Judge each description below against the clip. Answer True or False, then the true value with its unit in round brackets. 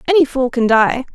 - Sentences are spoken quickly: True (210 wpm)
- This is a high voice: True (260 Hz)